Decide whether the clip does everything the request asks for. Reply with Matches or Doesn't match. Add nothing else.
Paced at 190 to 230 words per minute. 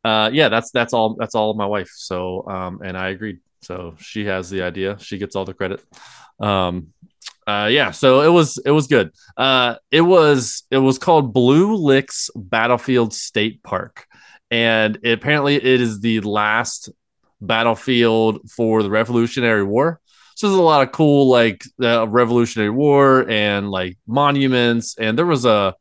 Doesn't match